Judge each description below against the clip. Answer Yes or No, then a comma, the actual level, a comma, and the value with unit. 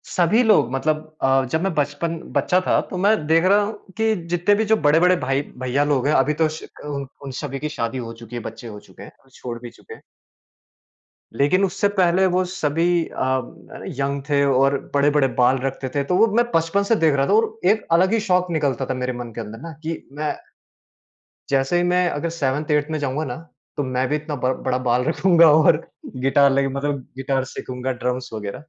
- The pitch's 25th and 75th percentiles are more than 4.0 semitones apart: Yes, average, 4.6 semitones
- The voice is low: No, medium, 145 Hz